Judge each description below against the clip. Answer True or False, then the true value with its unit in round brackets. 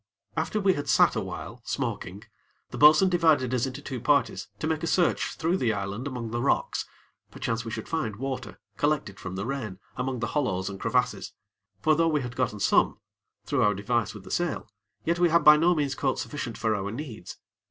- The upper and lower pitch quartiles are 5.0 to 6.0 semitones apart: True (5.4 semitones)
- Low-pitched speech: True (130 Hz)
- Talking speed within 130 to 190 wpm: False (205 wpm)